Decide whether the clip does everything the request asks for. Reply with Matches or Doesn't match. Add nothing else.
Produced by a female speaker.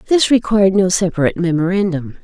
Matches